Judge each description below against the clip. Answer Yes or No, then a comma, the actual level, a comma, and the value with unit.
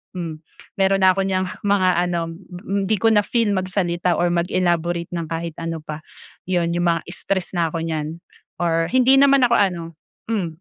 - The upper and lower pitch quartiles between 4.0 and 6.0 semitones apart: No, average, 2.7 semitones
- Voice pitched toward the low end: No, medium, 175 Hz